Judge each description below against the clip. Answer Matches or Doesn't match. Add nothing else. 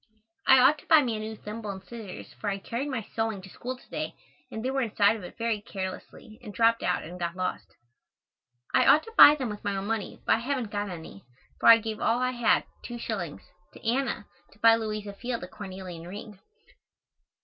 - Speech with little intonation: Doesn't match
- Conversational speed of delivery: Doesn't match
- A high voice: Matches